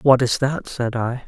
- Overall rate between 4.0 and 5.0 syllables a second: Yes, 4.3 syllables/s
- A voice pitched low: Yes, low, 125 Hz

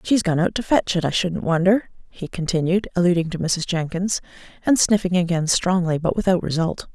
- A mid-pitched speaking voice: Yes, medium, 180 Hz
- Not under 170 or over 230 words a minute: Yes, average, 190 wpm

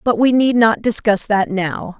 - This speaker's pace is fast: Yes, fast, 210 wpm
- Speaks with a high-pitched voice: Yes, high, 220 Hz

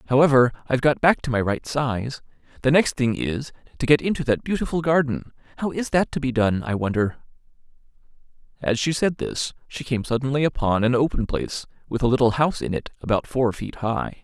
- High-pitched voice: No, low, 130 Hz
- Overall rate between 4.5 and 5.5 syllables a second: No, 5.7 syllables/s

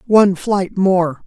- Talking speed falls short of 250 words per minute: Yes, average, 140 wpm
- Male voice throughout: No, female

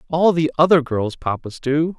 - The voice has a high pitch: No, medium, 150 Hz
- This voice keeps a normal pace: Yes, average, 180 wpm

